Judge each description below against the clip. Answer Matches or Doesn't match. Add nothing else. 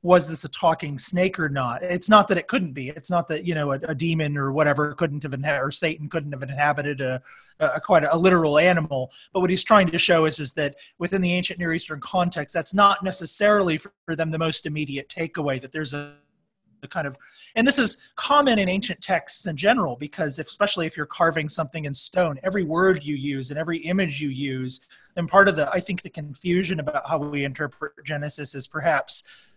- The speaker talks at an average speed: Doesn't match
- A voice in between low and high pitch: Matches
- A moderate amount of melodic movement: Matches